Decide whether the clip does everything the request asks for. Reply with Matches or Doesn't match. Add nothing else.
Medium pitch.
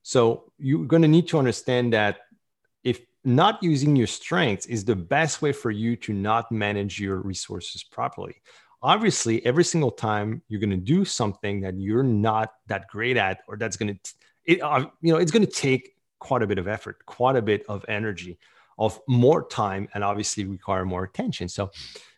Doesn't match